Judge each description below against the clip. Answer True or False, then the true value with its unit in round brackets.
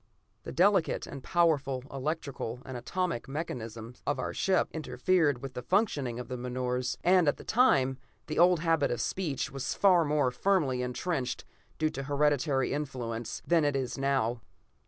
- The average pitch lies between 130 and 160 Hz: True (140 Hz)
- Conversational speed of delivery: True (160 wpm)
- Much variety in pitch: False (4.6 semitones)